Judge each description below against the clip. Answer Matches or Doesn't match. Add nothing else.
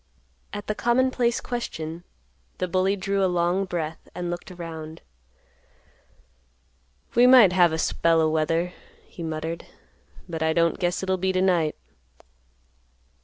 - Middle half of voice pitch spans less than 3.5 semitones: Matches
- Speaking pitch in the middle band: Matches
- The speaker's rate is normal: Doesn't match